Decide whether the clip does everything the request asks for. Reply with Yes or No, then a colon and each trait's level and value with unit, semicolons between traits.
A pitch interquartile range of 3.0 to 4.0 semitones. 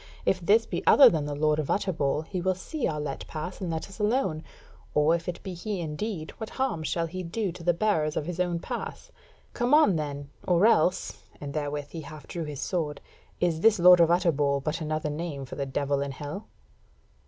Yes: average, 3.7 semitones